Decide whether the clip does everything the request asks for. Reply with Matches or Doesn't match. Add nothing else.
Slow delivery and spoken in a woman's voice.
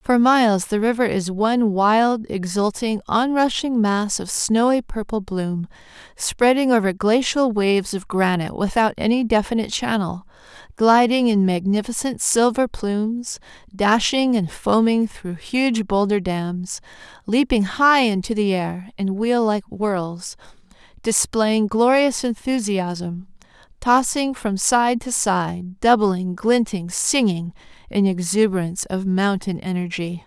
Matches